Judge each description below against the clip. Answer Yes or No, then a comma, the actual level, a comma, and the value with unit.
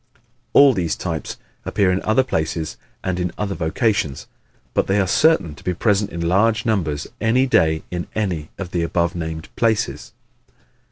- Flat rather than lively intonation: No, average, 4.7 semitones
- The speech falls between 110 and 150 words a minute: No, average, 165 wpm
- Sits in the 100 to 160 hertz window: No, very low, 90 Hz